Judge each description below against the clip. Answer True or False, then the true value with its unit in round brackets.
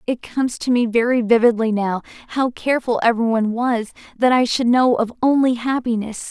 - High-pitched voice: True (235 Hz)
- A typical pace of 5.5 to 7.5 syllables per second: True (5.6 syllables/s)